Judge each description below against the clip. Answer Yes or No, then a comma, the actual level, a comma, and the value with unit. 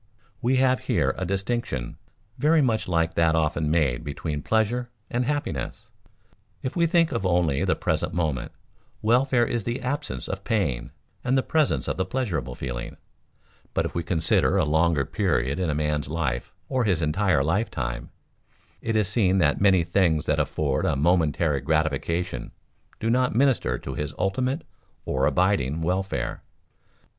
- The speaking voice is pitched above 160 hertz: No, very low, 90 Hz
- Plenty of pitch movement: Yes, wide, 7.7 semitones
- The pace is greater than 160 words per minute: No, average, 155 wpm